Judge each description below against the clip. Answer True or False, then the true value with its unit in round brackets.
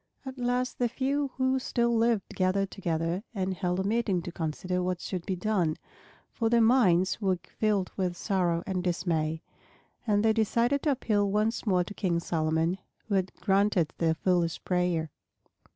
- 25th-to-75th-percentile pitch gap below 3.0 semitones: False (4.2 semitones)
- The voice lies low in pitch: False (190 Hz)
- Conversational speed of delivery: True (170 wpm)